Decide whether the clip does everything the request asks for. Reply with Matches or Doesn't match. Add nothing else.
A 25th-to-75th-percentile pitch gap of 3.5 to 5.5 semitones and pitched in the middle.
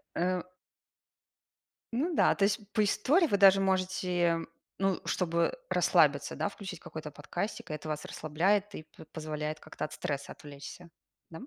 Matches